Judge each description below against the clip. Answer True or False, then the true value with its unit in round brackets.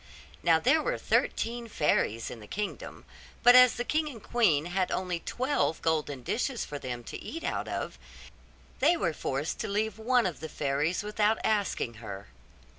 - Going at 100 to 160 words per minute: False (175 wpm)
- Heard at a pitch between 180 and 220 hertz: True (190 Hz)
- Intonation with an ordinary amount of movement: False (8.4 semitones)